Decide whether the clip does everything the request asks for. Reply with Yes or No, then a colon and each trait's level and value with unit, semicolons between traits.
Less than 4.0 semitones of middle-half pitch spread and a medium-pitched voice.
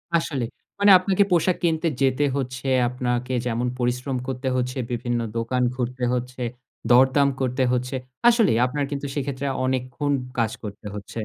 No: narrow, 2.4 semitones; low, 130 Hz